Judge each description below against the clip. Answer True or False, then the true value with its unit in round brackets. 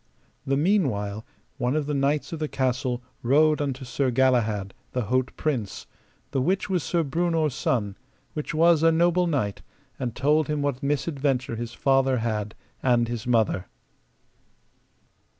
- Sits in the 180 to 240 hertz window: False (135 Hz)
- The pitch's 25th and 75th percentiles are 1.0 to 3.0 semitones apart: False (4.2 semitones)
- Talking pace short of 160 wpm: True (150 wpm)